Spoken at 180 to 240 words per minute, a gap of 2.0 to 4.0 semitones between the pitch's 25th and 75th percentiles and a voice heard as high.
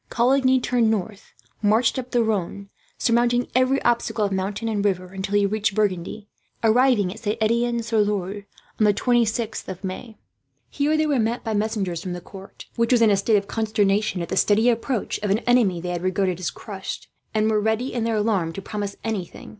Yes: average, 200 wpm; average, 2.9 semitones; high, 215 Hz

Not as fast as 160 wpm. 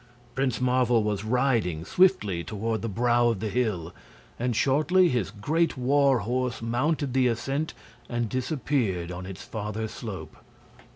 Yes: average, 140 wpm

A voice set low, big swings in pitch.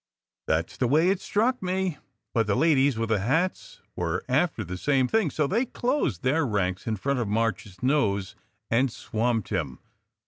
Yes: low, 125 Hz; wide, 7.5 semitones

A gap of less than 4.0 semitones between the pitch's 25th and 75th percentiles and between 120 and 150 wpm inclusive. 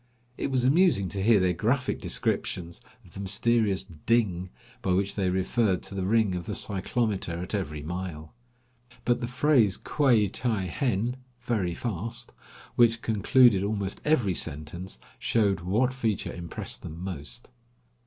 No: average, 4.5 semitones; average, 145 wpm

